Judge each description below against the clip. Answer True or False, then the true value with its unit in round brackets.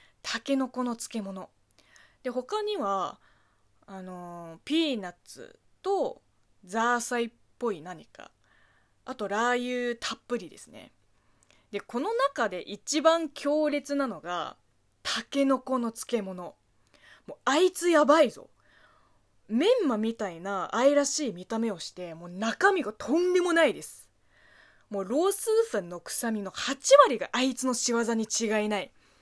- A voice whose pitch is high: True (240 Hz)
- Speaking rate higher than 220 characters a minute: True (255 characters per minute)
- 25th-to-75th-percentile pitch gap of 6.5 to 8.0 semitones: False (5.6 semitones)